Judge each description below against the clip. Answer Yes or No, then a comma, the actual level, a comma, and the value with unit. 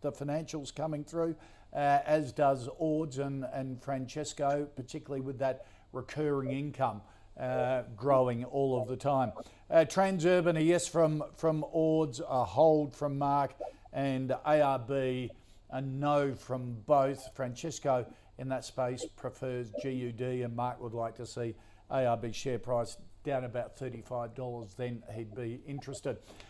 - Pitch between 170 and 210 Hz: No, low, 130 Hz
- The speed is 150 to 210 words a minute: No, average, 140 wpm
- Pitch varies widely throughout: No, average, 3.0 semitones